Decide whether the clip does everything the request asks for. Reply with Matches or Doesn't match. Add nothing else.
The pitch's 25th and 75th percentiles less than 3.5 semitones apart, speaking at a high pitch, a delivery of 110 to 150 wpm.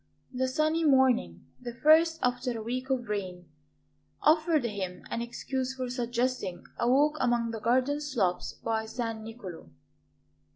Matches